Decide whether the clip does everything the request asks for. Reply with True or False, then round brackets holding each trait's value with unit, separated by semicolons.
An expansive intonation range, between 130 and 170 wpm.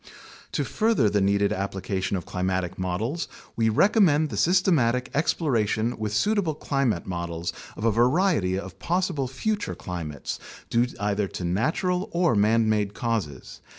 True (8.4 semitones; 140 wpm)